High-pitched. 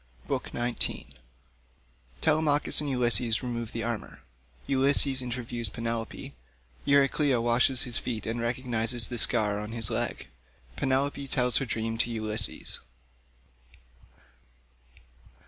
No: low, 115 Hz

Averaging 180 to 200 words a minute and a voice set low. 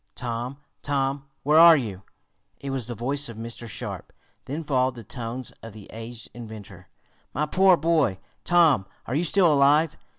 No: average, 165 wpm; low, 130 Hz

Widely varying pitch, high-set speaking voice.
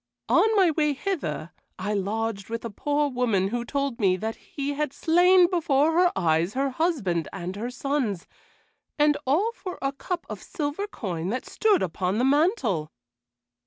Yes: wide, 8.0 semitones; very high, 270 Hz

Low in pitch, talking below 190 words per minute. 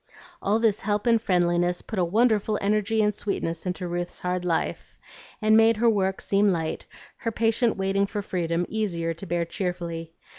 No: high, 195 Hz; average, 175 wpm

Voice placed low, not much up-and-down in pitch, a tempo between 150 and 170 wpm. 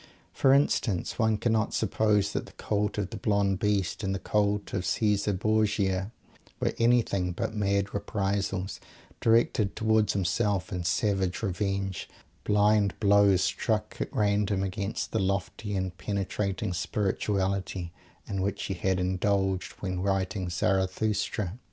No: low, 100 Hz; narrow, 1.8 semitones; slow, 135 wpm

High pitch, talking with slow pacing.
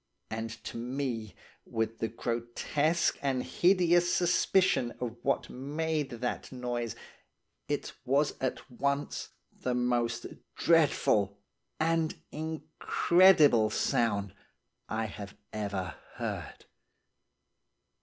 No: low, 125 Hz; slow, 95 wpm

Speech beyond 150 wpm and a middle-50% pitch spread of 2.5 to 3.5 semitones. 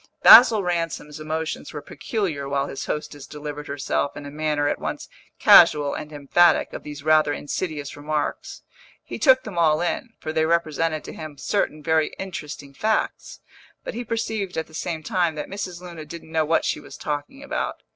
Yes: average, 180 wpm; average, 3.0 semitones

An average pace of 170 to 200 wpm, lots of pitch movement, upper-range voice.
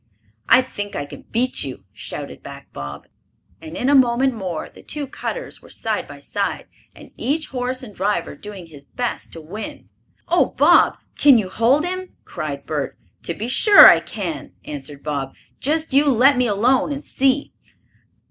Yes: average, 175 wpm; wide, 8.7 semitones; high, 235 Hz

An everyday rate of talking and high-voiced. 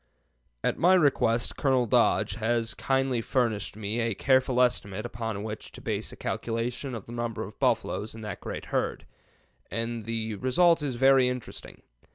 No: average, 165 wpm; low, 120 Hz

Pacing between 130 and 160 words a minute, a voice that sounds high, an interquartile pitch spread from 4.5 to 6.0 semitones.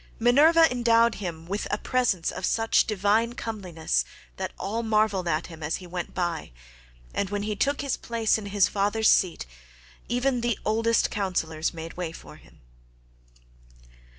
Yes: average, 155 wpm; high, 205 Hz; average, 4.8 semitones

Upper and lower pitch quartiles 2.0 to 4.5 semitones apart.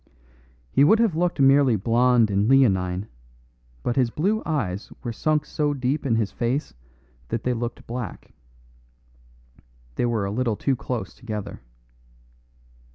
Yes: average, 4.1 semitones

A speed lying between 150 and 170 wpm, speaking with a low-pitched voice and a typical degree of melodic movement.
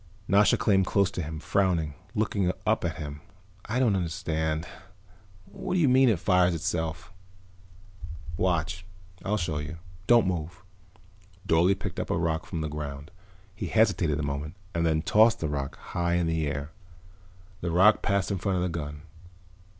Yes: average, 165 wpm; very low, 85 Hz; average, 3.9 semitones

